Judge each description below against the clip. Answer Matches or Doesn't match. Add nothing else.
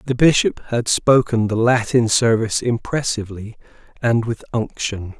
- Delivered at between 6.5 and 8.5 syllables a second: Doesn't match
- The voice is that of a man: Matches